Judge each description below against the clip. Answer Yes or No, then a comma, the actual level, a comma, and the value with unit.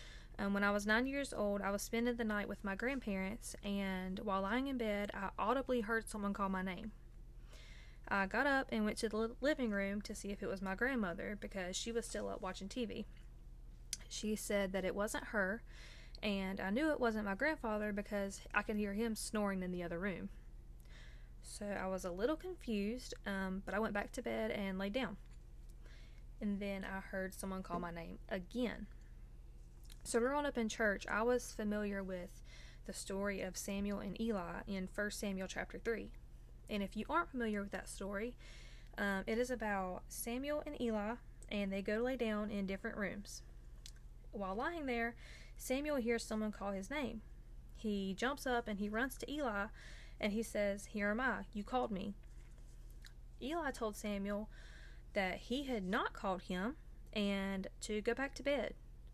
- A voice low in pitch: No, high, 210 Hz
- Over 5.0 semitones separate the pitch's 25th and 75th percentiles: No, average, 3.1 semitones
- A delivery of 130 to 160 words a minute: No, average, 185 wpm